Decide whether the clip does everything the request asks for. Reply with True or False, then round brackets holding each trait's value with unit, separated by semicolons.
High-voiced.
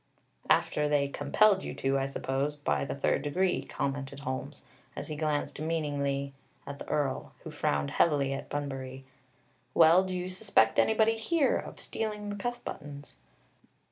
False (145 Hz)